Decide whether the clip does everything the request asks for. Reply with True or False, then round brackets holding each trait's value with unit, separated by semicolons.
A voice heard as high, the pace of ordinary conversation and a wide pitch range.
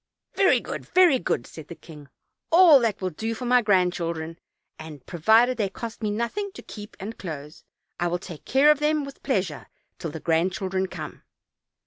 True (195 Hz; 180 wpm; 7.0 semitones)